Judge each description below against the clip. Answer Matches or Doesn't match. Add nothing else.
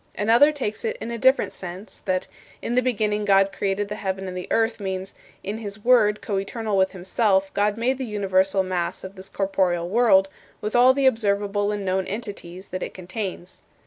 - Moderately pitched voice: Doesn't match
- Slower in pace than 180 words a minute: Doesn't match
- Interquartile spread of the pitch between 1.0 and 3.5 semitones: Matches